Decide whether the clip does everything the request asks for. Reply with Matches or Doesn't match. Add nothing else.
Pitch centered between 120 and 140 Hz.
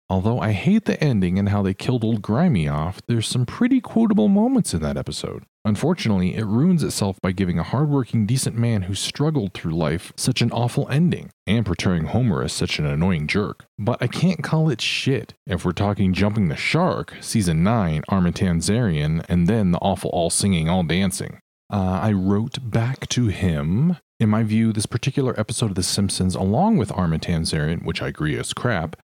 Doesn't match